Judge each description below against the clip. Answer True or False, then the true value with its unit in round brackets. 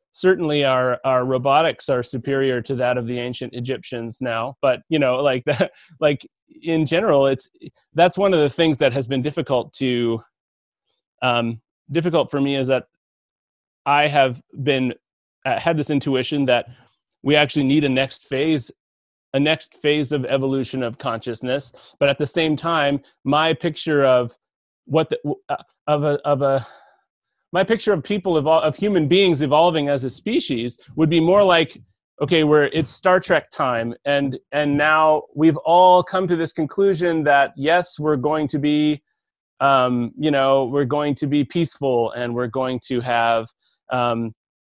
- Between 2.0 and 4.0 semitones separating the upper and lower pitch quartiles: True (3.7 semitones)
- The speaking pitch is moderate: True (145 Hz)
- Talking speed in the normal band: True (170 wpm)